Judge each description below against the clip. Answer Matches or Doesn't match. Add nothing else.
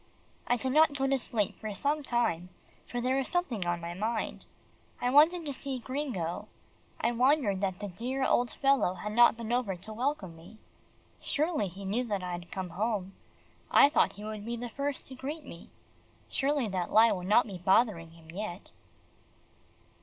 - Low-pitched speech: Doesn't match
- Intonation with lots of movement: Matches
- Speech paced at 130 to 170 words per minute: Doesn't match